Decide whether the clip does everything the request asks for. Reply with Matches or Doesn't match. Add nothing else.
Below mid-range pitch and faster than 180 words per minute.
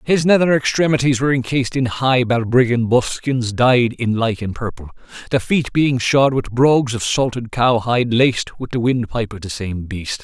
Doesn't match